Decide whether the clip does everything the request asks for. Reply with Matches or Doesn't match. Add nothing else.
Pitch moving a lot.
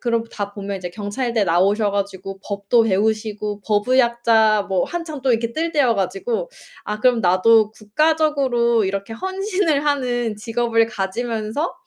Doesn't match